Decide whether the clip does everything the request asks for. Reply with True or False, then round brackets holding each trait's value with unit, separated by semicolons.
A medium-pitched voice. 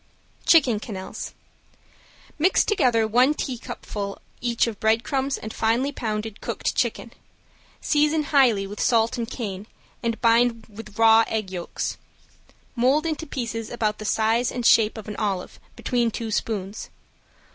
False (230 Hz)